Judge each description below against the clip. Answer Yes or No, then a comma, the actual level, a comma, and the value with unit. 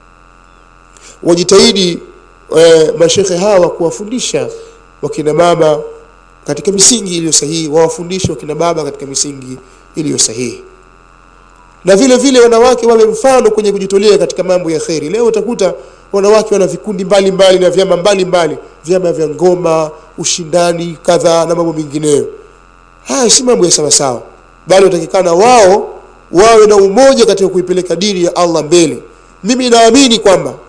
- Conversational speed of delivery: Yes, average, 130 wpm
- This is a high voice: No, medium, 180 Hz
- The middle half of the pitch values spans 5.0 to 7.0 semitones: Yes, wide, 5.6 semitones